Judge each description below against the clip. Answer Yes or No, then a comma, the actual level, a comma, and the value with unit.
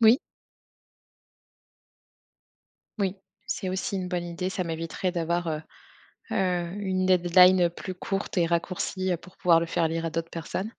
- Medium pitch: Yes, medium, 180 Hz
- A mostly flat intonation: Yes, narrow, 1.8 semitones